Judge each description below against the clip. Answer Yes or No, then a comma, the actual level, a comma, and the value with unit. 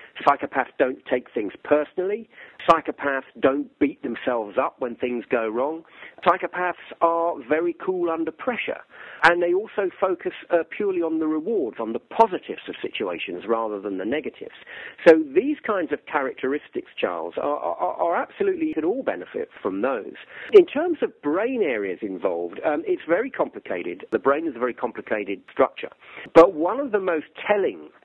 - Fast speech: No, average, 165 wpm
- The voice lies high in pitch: No, medium, 180 Hz